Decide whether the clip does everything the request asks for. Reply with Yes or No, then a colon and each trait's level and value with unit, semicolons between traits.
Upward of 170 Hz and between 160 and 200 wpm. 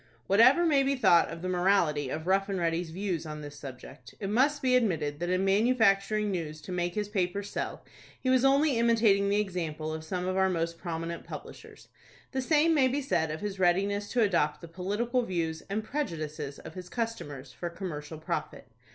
Yes: high, 190 Hz; average, 195 wpm